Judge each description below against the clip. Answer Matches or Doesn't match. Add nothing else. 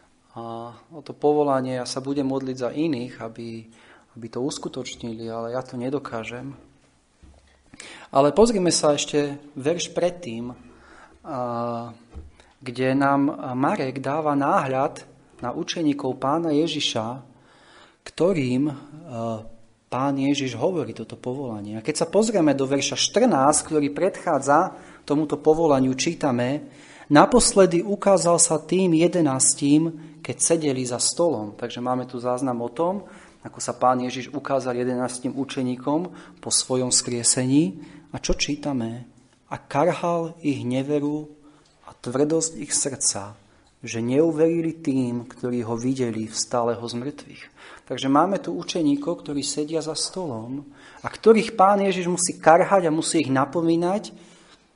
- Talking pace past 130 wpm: Doesn't match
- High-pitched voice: Doesn't match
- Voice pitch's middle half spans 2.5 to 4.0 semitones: Doesn't match